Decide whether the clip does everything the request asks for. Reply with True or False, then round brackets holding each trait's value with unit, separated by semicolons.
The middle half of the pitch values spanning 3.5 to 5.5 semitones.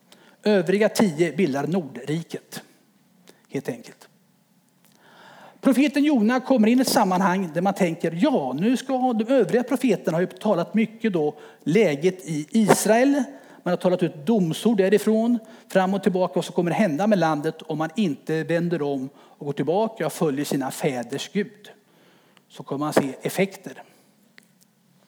True (4.3 semitones)